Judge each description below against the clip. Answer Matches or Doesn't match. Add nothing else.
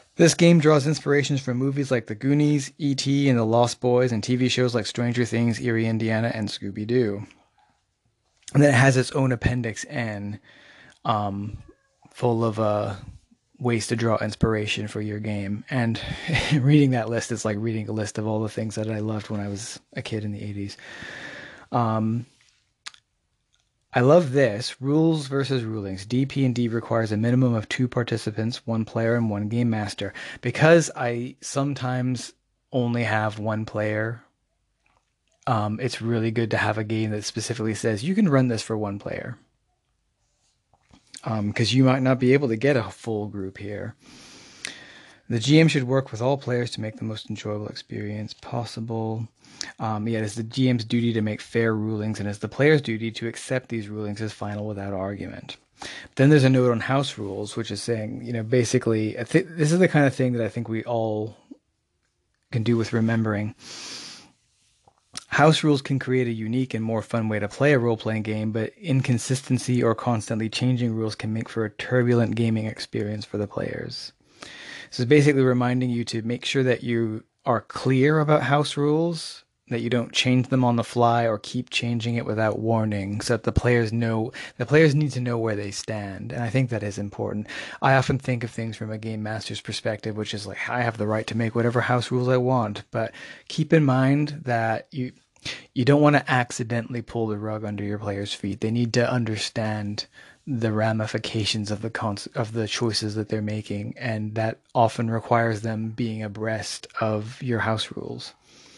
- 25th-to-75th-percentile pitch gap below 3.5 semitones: Matches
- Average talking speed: Matches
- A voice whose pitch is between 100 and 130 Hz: Matches